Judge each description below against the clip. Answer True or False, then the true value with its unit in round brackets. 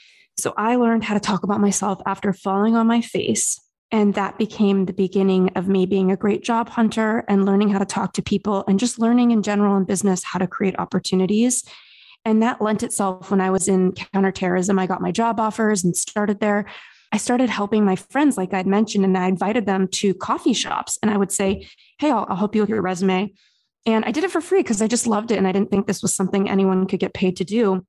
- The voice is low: False (200 Hz)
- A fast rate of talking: True (240 wpm)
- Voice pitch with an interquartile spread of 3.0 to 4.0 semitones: False (2.5 semitones)